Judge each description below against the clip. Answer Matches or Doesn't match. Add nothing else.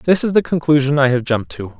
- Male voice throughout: Matches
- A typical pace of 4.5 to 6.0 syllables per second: Doesn't match